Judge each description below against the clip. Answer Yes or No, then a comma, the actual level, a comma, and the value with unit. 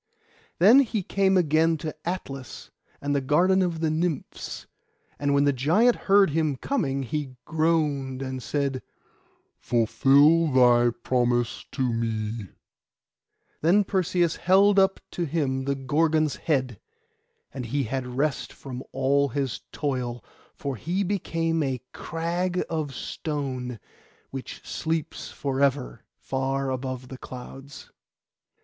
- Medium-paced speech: No, slow, 125 wpm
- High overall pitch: No, medium, 140 Hz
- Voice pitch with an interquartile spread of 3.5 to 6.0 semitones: Yes, average, 4.1 semitones